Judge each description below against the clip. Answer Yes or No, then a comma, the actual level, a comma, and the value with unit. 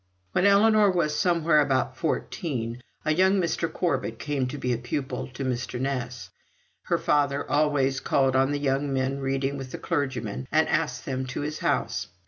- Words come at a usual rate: Yes, average, 170 wpm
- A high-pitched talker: No, medium, 140 Hz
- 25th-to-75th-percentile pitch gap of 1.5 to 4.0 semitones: Yes, average, 2.9 semitones